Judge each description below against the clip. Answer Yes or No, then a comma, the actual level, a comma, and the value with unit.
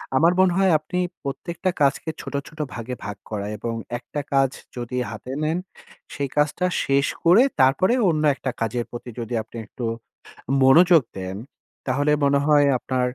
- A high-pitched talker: No, medium, 140 Hz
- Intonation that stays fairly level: No, average, 4.5 semitones